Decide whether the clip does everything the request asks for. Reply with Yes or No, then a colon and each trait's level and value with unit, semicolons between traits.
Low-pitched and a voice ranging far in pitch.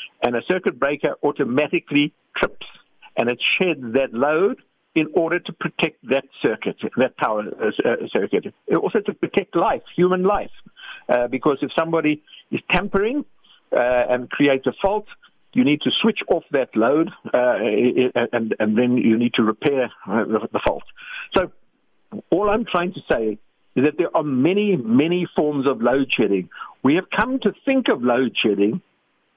No: medium, 155 Hz; wide, 8.2 semitones